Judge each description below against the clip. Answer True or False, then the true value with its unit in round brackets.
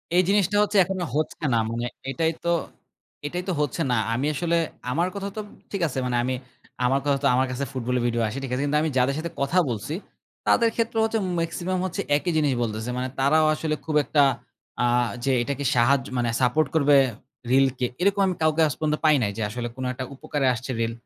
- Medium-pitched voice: True (145 Hz)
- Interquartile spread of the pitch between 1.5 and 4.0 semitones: False (4.8 semitones)